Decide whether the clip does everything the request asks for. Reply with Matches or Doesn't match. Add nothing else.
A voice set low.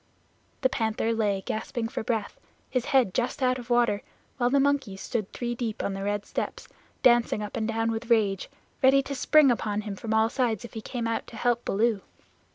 Doesn't match